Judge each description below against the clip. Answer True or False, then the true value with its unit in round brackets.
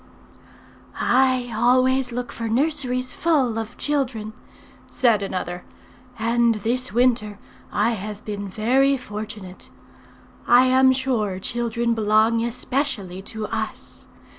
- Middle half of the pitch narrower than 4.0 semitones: True (3.1 semitones)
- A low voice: False (235 Hz)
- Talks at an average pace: False (110 wpm)